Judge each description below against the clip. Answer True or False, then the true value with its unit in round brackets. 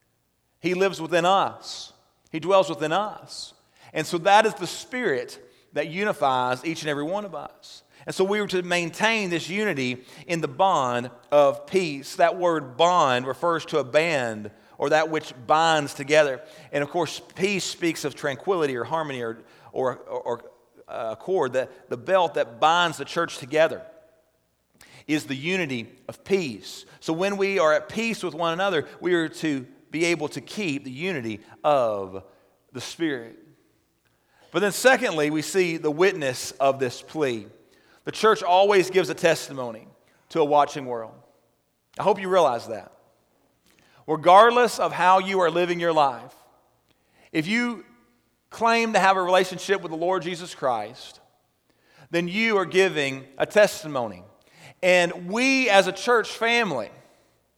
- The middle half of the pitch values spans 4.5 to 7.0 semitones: True (4.9 semitones)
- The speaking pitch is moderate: True (165 Hz)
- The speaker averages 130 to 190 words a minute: True (160 wpm)